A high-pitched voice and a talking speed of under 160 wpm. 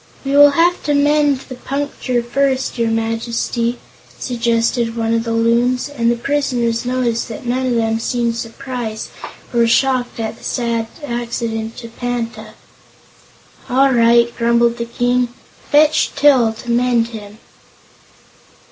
Yes: high, 235 Hz; average, 140 wpm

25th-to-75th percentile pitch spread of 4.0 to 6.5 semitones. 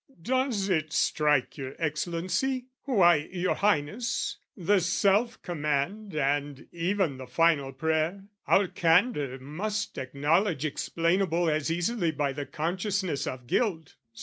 Yes: average, 5.1 semitones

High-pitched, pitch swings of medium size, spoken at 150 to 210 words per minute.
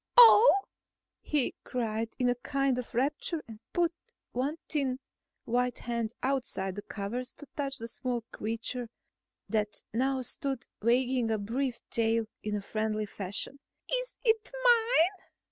No: very high, 250 Hz; average, 3.8 semitones; slow, 135 wpm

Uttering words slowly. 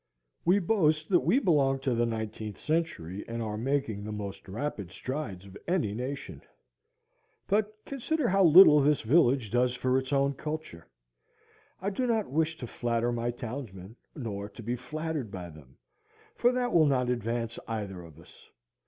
No: average, 165 wpm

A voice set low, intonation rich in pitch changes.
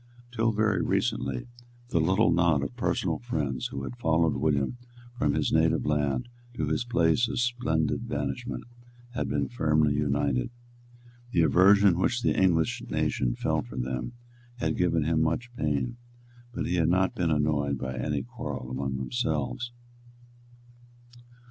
Yes: very low, 80 Hz; wide, 6.4 semitones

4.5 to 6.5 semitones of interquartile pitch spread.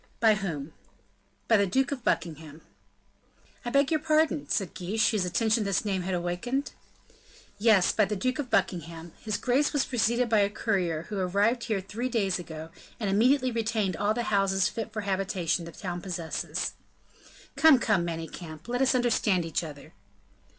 Yes: average, 5.0 semitones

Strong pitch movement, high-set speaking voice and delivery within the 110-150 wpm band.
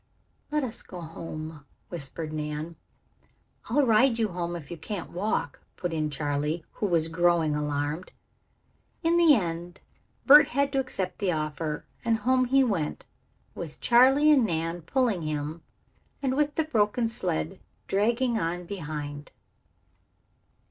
No: wide, 7.5 semitones; medium, 175 Hz; average, 140 wpm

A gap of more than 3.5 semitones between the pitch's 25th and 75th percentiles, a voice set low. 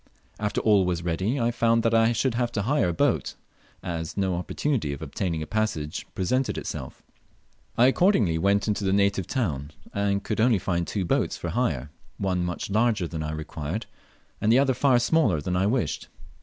Yes: average, 5.2 semitones; low, 100 Hz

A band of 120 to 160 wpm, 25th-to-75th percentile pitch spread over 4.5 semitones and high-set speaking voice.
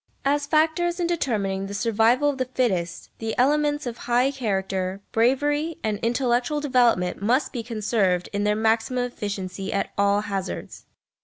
Yes: average, 150 wpm; average, 5.1 semitones; high, 235 Hz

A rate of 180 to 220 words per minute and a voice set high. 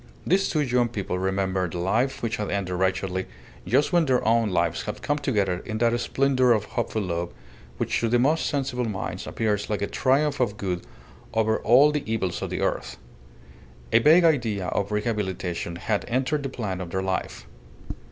No: average, 185 wpm; low, 110 Hz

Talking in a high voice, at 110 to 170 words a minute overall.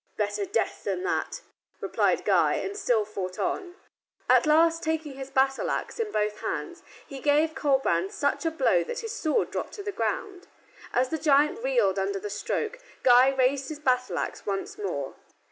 No: very high, 285 Hz; average, 180 wpm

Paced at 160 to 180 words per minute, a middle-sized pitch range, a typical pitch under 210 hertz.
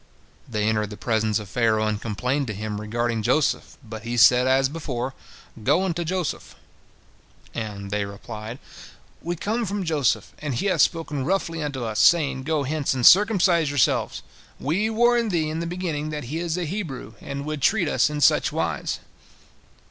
No: average, 175 wpm; wide, 6.7 semitones; medium, 140 Hz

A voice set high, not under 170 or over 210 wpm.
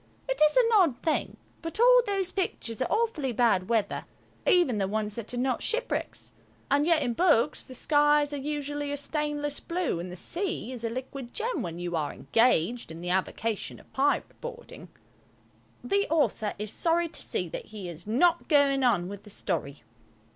Yes: very high, 275 Hz; average, 185 wpm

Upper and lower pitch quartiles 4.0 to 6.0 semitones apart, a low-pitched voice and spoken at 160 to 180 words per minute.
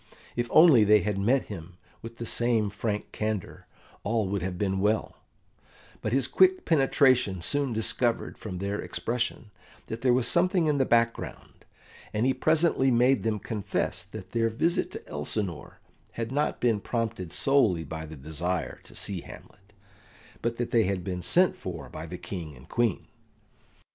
Yes: average, 4.7 semitones; low, 110 Hz; average, 165 wpm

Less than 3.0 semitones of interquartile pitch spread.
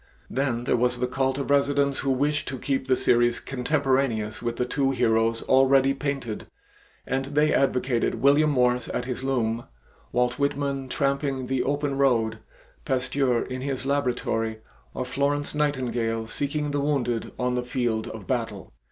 Yes: narrow, 2.4 semitones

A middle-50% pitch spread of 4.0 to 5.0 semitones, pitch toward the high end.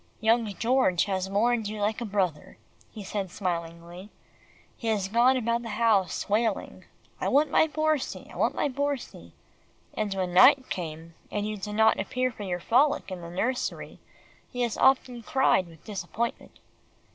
Yes: average, 4.4 semitones; high, 215 Hz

